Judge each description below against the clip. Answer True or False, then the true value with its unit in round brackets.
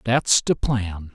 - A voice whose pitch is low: True (105 Hz)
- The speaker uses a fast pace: False (155 wpm)